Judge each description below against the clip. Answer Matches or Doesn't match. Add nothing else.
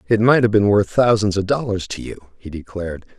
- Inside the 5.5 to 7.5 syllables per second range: Matches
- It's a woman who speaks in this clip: Doesn't match